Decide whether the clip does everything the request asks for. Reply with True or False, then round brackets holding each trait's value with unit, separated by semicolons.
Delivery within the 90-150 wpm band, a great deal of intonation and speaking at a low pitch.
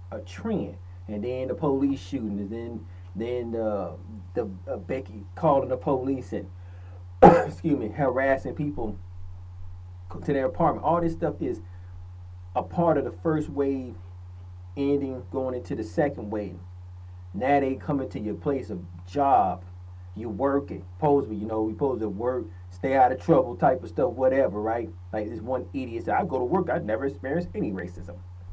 False (170 wpm; 6.5 semitones; 105 Hz)